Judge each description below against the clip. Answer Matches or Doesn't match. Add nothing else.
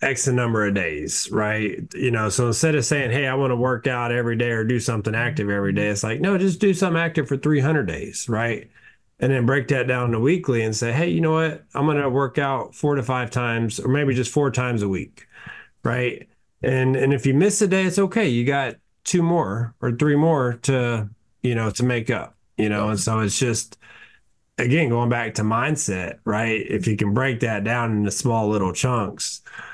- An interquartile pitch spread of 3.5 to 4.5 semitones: Matches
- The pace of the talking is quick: Matches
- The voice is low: Matches